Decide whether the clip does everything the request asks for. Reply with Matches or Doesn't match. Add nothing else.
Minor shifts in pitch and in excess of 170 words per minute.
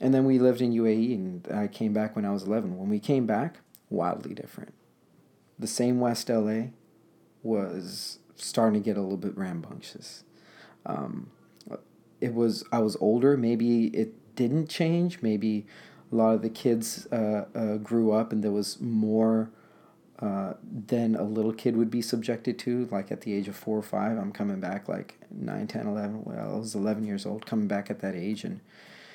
Matches